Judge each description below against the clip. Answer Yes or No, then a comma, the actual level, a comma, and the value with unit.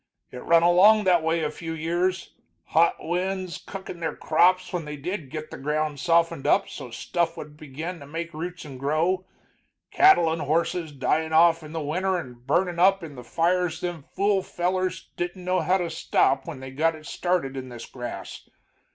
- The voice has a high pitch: No, medium, 165 Hz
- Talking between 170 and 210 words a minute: Yes, average, 185 wpm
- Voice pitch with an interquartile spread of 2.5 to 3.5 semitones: Yes, average, 3.0 semitones